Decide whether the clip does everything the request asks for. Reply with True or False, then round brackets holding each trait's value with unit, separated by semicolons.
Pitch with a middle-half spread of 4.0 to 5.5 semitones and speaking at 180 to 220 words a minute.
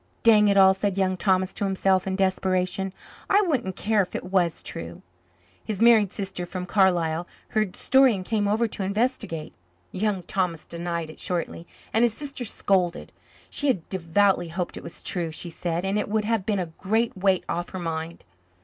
False (3.1 semitones; 190 wpm)